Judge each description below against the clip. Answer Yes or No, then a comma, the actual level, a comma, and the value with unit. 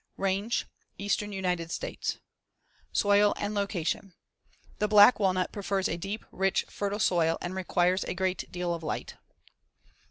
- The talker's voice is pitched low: No, high, 190 Hz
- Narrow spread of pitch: Yes, narrow, 2.2 semitones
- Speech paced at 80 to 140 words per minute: Yes, slow, 135 wpm